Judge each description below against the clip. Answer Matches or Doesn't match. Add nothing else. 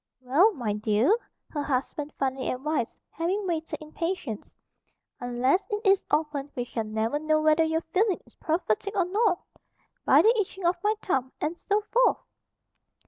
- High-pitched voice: Matches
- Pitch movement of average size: Doesn't match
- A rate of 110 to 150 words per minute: Doesn't match